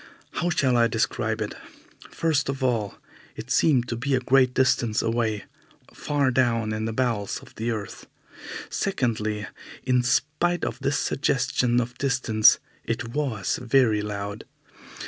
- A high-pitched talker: No, low, 125 Hz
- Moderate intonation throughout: Yes, average, 3.3 semitones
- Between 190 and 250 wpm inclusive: No, average, 145 wpm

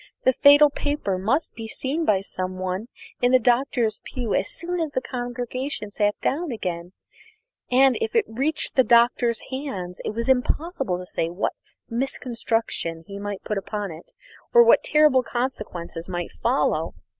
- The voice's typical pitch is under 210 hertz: No, high, 240 Hz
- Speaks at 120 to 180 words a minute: Yes, average, 165 wpm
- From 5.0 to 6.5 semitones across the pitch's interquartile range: Yes, wide, 5.5 semitones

